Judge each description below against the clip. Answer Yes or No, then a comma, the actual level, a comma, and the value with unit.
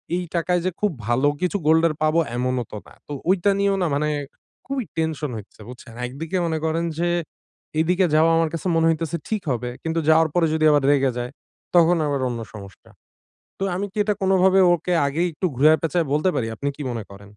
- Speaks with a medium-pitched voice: Yes, medium, 160 Hz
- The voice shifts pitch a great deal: No, average, 4.2 semitones